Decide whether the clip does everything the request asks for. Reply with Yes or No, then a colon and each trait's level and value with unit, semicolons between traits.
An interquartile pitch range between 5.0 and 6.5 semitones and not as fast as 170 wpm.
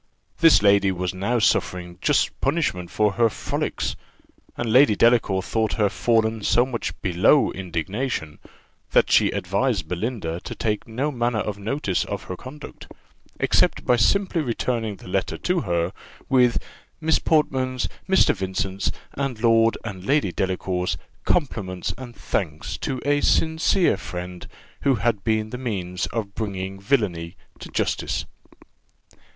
Yes: average, 5.3 semitones; average, 140 wpm